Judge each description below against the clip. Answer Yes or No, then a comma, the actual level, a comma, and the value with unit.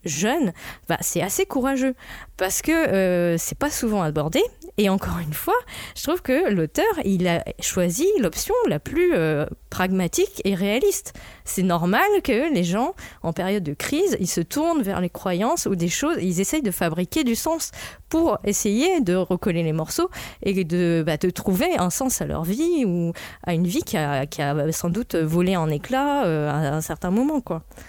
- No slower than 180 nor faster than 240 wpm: Yes, average, 190 wpm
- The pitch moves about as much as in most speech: No, wide, 8.7 semitones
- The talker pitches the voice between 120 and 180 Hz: No, high, 190 Hz